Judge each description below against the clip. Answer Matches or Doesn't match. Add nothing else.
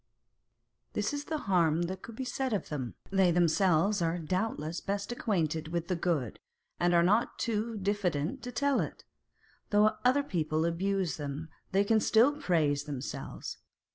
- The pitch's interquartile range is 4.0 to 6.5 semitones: Matches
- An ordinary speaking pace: Matches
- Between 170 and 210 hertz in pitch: Matches